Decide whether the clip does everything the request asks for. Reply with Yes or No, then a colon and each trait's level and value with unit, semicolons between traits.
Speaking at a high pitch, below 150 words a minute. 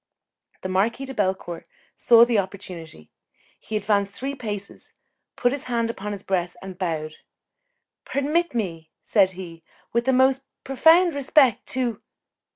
Yes: high, 210 Hz; average, 140 wpm